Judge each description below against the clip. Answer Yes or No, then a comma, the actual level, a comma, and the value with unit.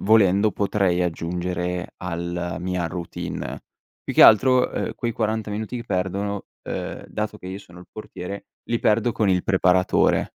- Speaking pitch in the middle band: No, very low, 95 Hz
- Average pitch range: Yes, average, 3.2 semitones